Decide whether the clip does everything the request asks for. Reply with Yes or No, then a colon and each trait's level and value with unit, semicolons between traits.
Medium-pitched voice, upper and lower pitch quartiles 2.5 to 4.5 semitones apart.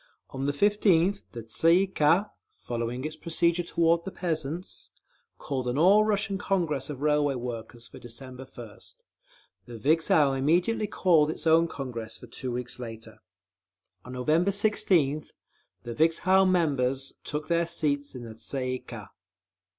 No: medium, 150 Hz; average, 5.2 semitones